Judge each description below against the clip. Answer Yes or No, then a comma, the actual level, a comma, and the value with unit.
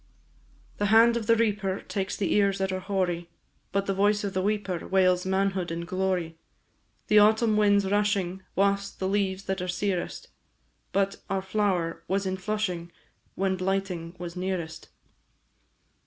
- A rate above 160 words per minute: No, average, 155 wpm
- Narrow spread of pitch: Yes, narrow, 1.8 semitones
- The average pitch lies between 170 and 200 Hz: Yes, high, 190 Hz